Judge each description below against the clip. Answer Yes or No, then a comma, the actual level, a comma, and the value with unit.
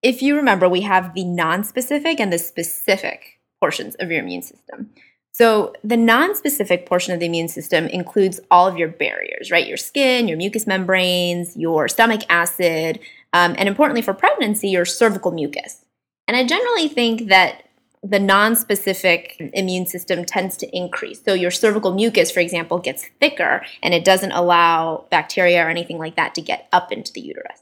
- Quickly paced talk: No, average, 175 wpm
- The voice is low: No, high, 190 Hz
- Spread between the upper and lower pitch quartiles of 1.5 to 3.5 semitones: No, average, 4.5 semitones